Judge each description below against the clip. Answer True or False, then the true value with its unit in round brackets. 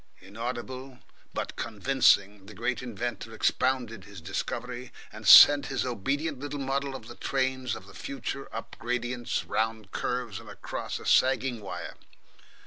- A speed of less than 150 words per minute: True (140 wpm)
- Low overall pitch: True (120 Hz)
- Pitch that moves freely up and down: False (3.4 semitones)